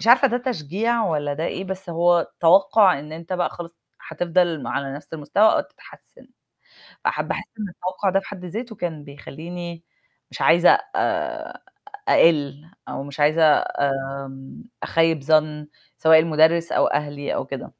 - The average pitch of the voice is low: No, medium, 165 Hz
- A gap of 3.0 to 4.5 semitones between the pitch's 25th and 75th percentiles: Yes, average, 3.7 semitones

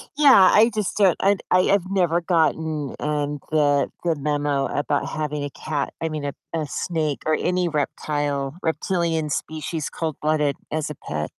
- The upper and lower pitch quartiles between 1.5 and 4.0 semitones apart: Yes, average, 2.7 semitones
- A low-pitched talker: No, medium, 155 Hz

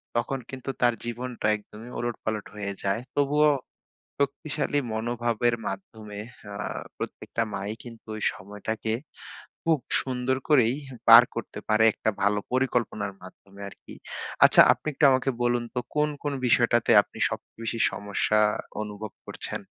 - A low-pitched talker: Yes, low, 115 Hz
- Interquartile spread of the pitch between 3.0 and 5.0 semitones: Yes, average, 3.3 semitones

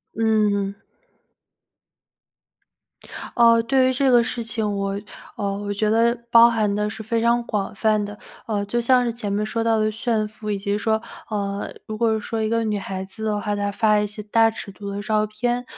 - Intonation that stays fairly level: Yes, narrow, 1.9 semitones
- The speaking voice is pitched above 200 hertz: Yes, high, 215 Hz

